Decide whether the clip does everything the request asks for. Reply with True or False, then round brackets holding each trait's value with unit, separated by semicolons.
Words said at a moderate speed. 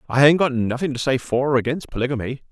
False (240 wpm)